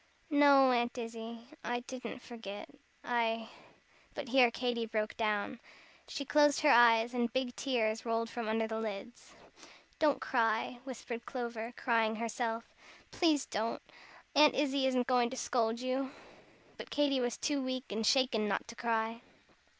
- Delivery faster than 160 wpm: No, average, 150 wpm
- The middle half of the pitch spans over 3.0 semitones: No, narrow, 2.5 semitones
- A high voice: Yes, high, 240 Hz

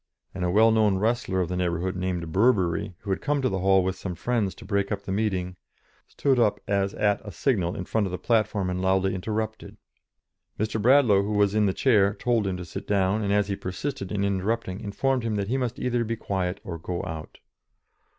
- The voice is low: Yes, low, 100 Hz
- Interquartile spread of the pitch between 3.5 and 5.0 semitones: No, average, 2.9 semitones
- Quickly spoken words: Yes, fast, 220 wpm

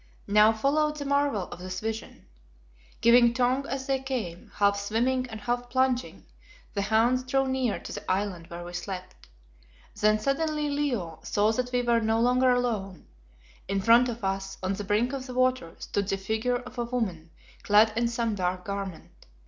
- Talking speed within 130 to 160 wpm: No, average, 180 wpm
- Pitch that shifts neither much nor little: Yes, average, 4.2 semitones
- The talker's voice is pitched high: Yes, high, 230 Hz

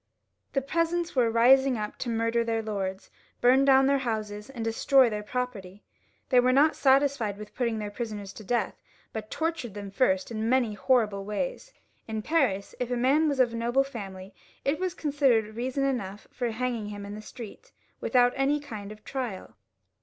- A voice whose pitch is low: No, high, 235 Hz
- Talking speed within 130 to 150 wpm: No, average, 180 wpm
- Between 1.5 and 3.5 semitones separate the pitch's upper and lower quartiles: No, average, 4.2 semitones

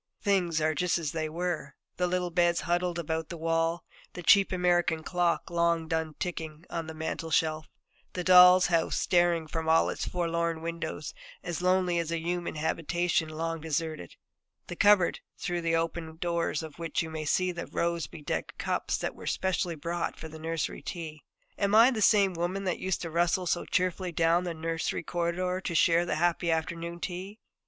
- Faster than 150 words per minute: Yes, average, 180 wpm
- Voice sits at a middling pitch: Yes, medium, 170 Hz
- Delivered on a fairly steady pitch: Yes, narrow, 1.6 semitones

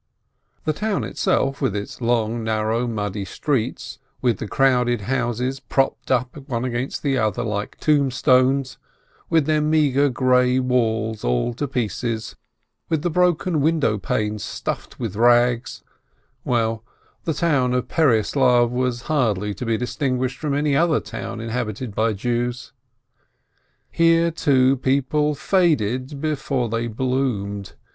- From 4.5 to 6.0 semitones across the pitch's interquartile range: No, average, 3.6 semitones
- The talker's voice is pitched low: Yes, low, 125 Hz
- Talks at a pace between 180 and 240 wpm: No, slow, 135 wpm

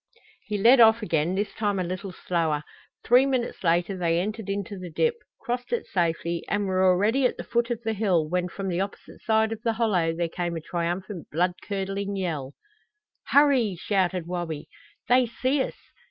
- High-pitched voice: Yes, high, 195 Hz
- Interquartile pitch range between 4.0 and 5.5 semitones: Yes, average, 4.3 semitones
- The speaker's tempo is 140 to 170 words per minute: No, average, 185 wpm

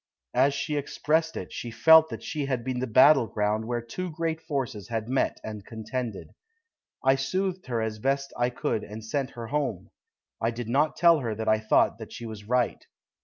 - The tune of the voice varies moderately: Yes, average, 4.5 semitones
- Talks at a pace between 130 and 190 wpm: No, average, 200 wpm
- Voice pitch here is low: Yes, low, 125 Hz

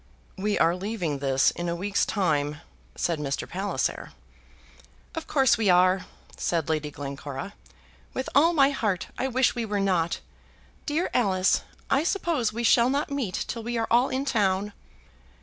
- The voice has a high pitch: Yes, high, 205 Hz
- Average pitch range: No, wide, 6.8 semitones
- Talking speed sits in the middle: Yes, average, 160 wpm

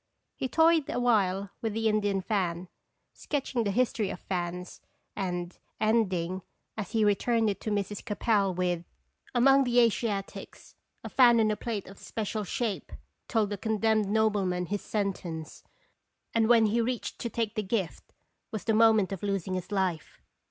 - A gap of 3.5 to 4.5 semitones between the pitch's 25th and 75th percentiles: No, average, 3.0 semitones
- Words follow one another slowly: No, average, 165 wpm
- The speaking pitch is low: No, high, 210 Hz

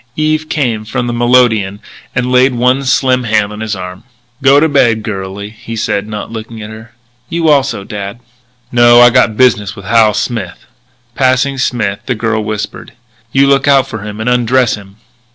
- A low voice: Yes, low, 115 Hz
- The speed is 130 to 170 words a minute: No, average, 180 wpm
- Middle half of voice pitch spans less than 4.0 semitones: Yes, average, 3.3 semitones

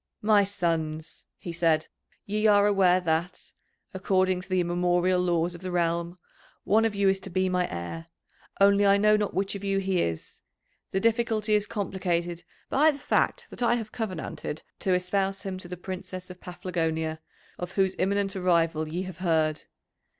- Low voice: No, medium, 185 Hz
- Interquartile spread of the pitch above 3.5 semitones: No, narrow, 2.6 semitones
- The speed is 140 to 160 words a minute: No, average, 175 wpm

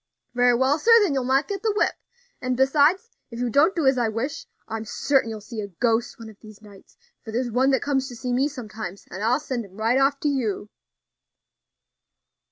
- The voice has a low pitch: No, very high, 250 Hz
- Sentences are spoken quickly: Yes, fast, 210 wpm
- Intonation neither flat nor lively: Yes, average, 4.0 semitones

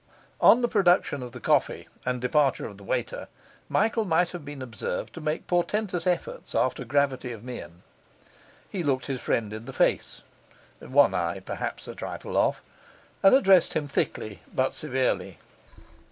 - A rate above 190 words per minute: No, average, 155 wpm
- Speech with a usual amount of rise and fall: No, wide, 6.4 semitones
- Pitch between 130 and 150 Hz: Yes, medium, 140 Hz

